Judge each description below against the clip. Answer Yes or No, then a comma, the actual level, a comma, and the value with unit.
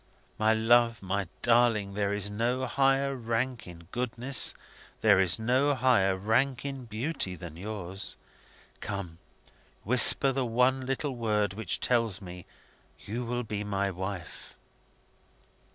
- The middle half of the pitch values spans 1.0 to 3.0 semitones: No, average, 4.1 semitones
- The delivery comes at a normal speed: No, slow, 130 wpm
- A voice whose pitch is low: Yes, low, 110 Hz